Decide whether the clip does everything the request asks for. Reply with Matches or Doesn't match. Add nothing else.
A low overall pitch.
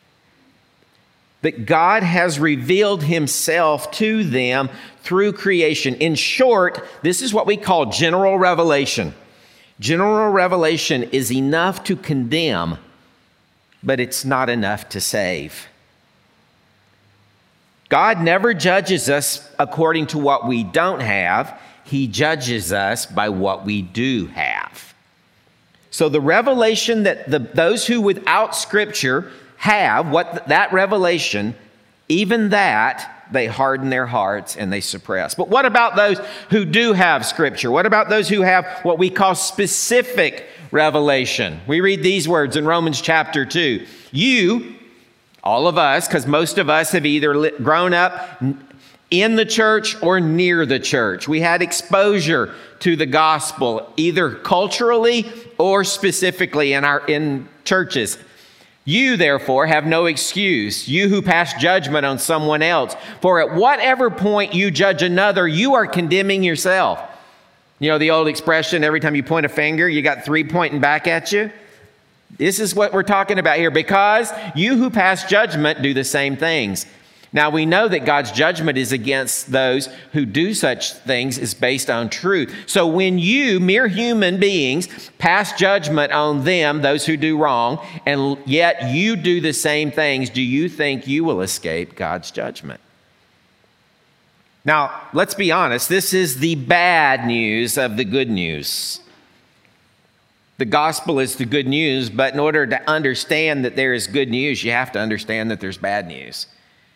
Doesn't match